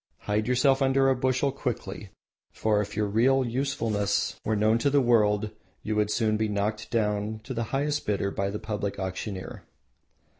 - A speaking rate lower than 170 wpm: No, average, 175 wpm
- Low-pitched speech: Yes, low, 110 Hz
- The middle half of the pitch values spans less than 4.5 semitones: Yes, average, 3.8 semitones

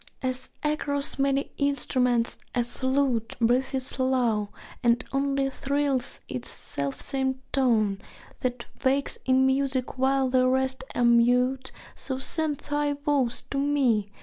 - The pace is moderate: No, slow, 120 wpm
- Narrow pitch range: Yes, narrow, 2.1 semitones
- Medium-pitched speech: No, very high, 260 Hz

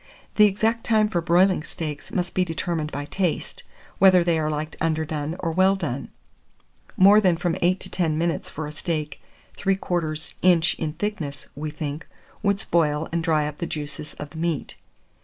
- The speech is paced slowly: No, average, 175 wpm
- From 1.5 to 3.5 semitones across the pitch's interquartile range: Yes, average, 3.2 semitones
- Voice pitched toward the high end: No, medium, 165 Hz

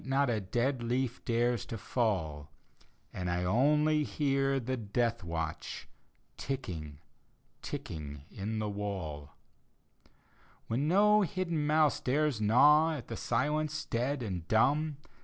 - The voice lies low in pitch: Yes, low, 120 Hz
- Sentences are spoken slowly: Yes, slow, 125 wpm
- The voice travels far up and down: Yes, wide, 6.6 semitones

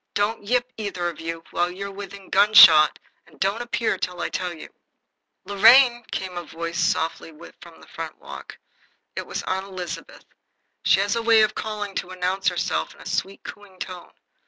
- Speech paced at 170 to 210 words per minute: Yes, average, 180 wpm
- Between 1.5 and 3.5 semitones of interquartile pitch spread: Yes, average, 3.0 semitones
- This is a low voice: No, high, 190 Hz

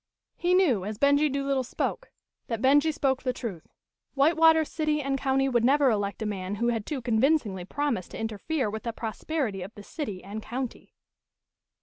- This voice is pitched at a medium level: No, very high, 255 Hz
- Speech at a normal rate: Yes, average, 185 wpm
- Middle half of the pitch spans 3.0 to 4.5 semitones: No, average, 5.1 semitones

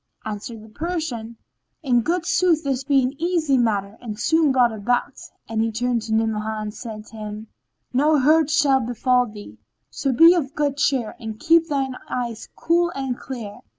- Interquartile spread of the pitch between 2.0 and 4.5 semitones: No, average, 5.1 semitones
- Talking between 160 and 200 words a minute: Yes, average, 180 wpm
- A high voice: Yes, very high, 250 Hz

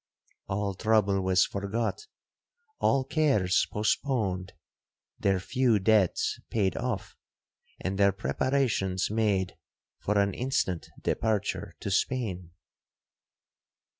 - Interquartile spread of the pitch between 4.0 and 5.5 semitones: Yes, average, 4.4 semitones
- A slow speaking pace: Yes, slow, 80 wpm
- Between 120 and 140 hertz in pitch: No, low, 105 Hz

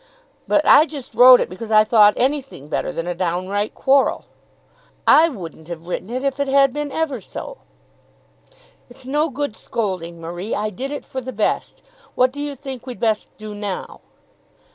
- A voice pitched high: Yes, high, 245 Hz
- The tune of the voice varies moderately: No, wide, 5.8 semitones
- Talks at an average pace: Yes, average, 180 wpm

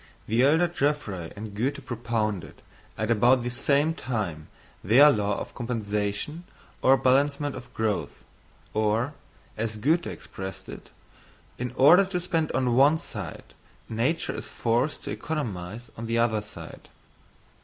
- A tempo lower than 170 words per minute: Yes, average, 140 wpm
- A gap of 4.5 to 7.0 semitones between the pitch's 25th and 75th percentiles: Yes, average, 5.1 semitones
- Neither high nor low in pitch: No, low, 120 Hz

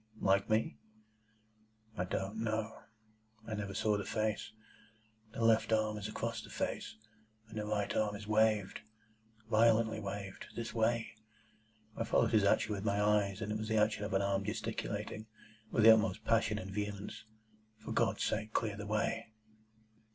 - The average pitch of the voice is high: No, low, 110 Hz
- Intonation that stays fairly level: Yes, narrow, 1.3 semitones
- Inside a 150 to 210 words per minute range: Yes, average, 160 wpm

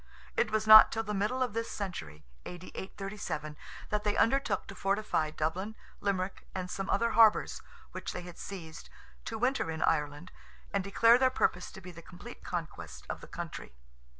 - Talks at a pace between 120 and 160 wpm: No, average, 180 wpm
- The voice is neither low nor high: No, high, 195 Hz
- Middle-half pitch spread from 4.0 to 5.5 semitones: Yes, average, 4.4 semitones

